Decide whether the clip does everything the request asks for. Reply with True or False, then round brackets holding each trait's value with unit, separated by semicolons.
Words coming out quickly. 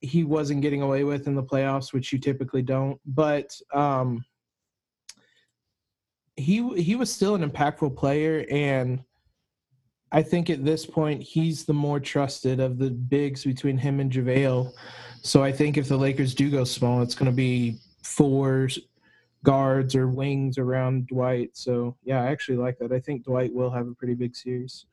False (175 wpm)